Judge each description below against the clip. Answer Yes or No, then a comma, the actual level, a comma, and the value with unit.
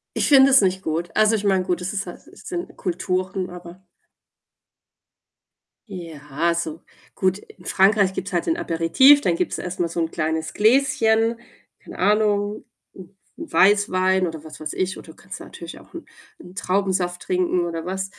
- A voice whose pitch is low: No, medium, 185 Hz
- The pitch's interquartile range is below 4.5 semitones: Yes, average, 3.1 semitones